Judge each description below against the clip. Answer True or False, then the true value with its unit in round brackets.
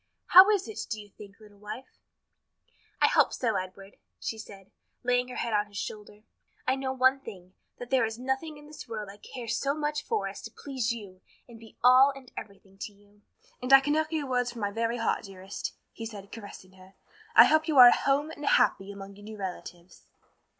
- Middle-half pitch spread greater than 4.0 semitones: True (4.7 semitones)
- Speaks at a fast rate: True (215 wpm)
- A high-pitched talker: True (230 Hz)